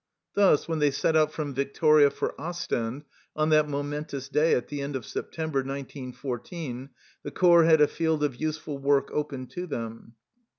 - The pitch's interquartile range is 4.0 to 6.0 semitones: No, narrow, 2.4 semitones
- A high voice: No, medium, 145 Hz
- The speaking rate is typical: Yes, average, 170 wpm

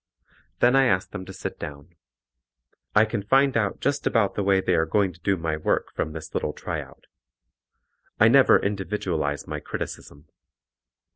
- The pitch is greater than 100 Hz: No, very low, 95 Hz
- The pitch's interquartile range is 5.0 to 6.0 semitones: Yes, average, 5.3 semitones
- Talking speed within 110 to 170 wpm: Yes, average, 165 wpm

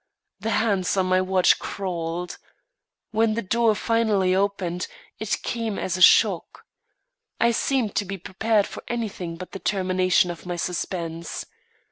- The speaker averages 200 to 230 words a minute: No, average, 145 wpm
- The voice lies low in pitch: No, high, 190 Hz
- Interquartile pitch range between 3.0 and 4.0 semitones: Yes, average, 3.3 semitones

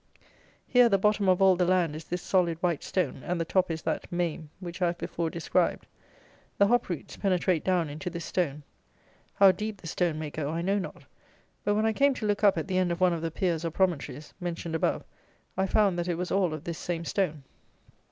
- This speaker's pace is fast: Yes, fast, 230 wpm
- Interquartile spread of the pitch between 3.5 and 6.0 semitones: No, narrow, 2.6 semitones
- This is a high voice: No, medium, 175 Hz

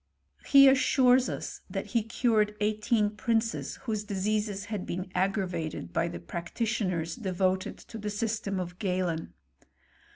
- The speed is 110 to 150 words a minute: Yes, slow, 135 wpm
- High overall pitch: Yes, high, 205 Hz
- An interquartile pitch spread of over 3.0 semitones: Yes, average, 3.4 semitones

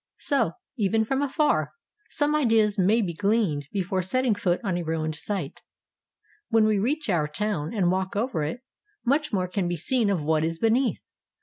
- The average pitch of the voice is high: Yes, high, 205 Hz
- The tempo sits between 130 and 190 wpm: Yes, average, 180 wpm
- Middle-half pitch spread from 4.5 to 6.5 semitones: Yes, average, 5.1 semitones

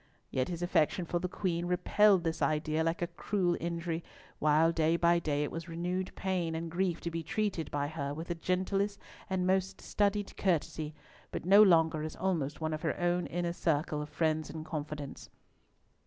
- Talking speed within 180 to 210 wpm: Yes, average, 185 wpm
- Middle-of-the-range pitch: Yes, medium, 170 Hz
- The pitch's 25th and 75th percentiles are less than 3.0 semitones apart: Yes, narrow, 2.5 semitones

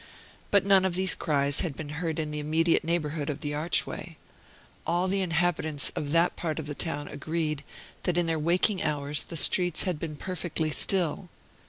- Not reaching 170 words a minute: No, average, 185 wpm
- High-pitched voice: No, medium, 160 Hz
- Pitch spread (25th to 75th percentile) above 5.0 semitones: No, average, 2.8 semitones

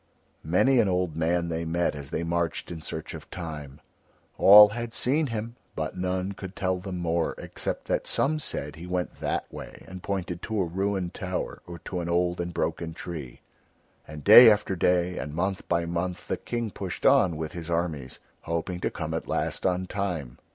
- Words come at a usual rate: Yes, average, 195 wpm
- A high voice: No, very low, 90 Hz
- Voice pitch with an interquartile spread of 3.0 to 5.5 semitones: No, narrow, 2.6 semitones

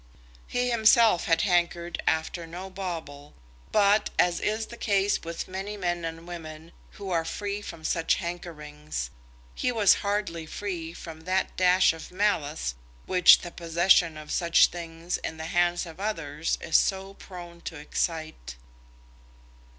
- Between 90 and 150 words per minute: Yes, average, 145 wpm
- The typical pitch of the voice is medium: Yes, medium, 175 Hz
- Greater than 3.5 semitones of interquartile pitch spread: No, average, 2.9 semitones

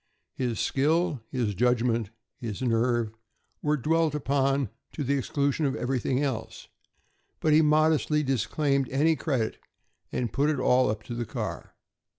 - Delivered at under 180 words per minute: Yes, average, 145 wpm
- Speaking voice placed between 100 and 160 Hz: Yes, low, 135 Hz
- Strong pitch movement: No, average, 3.8 semitones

